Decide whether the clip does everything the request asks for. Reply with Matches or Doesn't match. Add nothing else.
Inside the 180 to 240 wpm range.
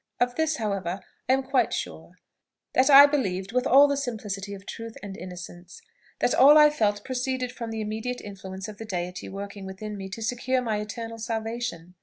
Matches